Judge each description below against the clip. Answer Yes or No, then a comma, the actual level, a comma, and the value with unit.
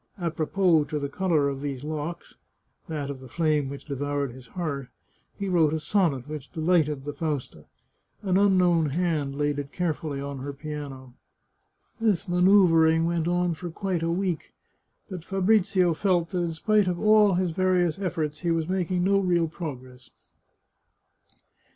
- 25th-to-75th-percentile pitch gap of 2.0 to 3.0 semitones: No, average, 3.8 semitones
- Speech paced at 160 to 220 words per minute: Yes, average, 170 wpm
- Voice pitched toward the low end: No, medium, 165 Hz